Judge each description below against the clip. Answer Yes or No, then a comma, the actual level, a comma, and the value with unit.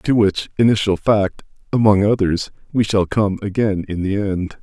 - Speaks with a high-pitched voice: No, low, 100 Hz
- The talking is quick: No, average, 170 wpm